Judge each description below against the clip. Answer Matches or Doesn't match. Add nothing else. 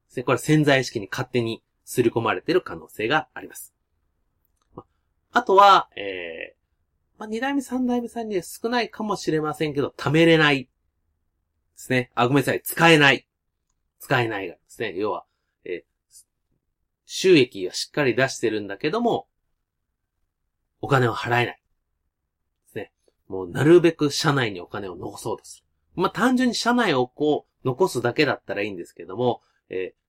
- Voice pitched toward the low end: Doesn't match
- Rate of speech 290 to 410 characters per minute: Matches